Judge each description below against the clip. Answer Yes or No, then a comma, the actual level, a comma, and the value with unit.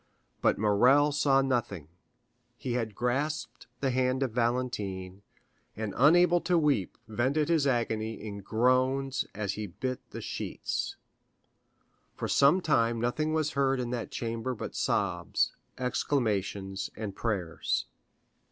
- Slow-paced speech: Yes, slow, 125 wpm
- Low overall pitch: Yes, low, 125 Hz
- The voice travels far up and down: No, average, 4.1 semitones